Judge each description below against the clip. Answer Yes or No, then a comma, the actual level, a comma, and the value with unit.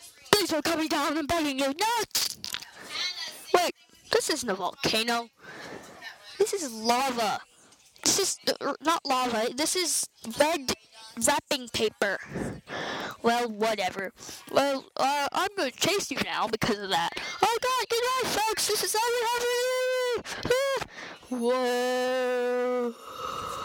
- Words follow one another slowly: Yes, slow, 115 wpm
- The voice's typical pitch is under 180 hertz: No, very high, 295 Hz